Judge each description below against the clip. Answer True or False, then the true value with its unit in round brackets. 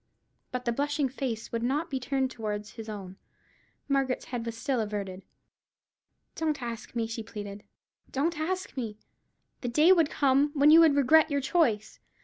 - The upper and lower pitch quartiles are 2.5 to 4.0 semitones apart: False (4.6 semitones)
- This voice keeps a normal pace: True (165 wpm)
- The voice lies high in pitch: True (260 Hz)